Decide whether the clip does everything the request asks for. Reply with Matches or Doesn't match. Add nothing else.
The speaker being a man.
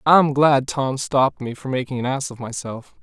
Matches